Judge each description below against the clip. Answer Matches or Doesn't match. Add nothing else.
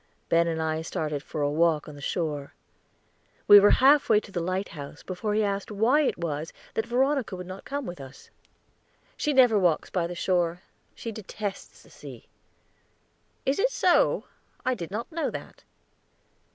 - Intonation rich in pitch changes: Matches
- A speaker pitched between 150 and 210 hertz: Matches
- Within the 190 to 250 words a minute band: Doesn't match